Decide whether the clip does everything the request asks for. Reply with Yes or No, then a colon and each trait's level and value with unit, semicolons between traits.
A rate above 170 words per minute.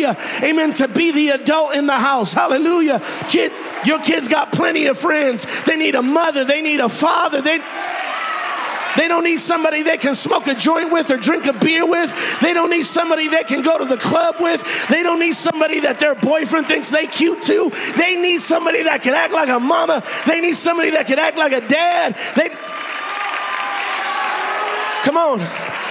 Yes: average, 190 wpm